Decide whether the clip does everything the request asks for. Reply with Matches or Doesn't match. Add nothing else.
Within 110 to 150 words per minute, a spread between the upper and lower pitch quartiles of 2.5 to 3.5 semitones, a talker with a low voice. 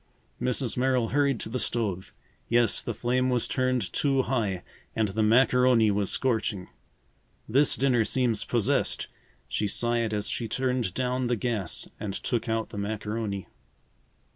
Matches